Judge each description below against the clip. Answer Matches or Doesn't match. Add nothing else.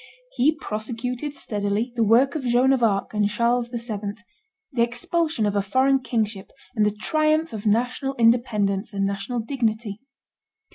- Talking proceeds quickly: Doesn't match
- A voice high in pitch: Matches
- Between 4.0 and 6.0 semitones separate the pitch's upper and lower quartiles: Doesn't match